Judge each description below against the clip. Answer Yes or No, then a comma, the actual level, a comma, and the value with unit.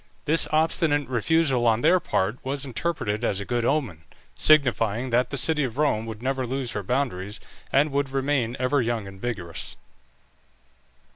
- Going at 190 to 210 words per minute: No, average, 160 wpm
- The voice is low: Yes, low, 130 Hz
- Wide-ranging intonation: No, average, 4.1 semitones